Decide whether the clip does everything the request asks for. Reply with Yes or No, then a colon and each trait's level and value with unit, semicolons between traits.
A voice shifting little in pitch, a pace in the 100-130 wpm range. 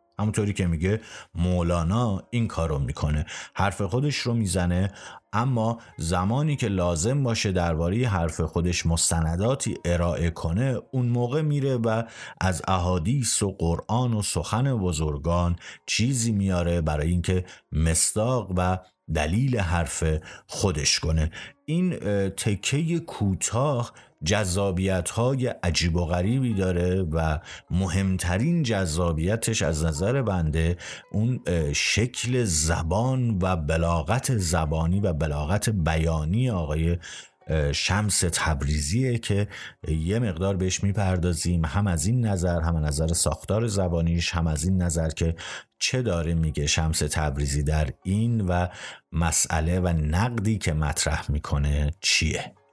No: average, 5.1 semitones; average, 120 wpm